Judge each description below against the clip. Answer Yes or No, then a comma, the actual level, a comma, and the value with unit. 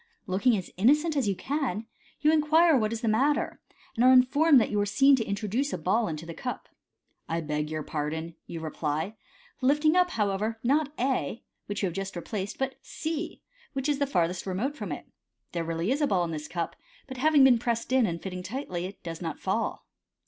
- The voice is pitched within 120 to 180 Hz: No, high, 220 Hz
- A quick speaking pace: Yes, fast, 215 wpm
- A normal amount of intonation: No, wide, 7.6 semitones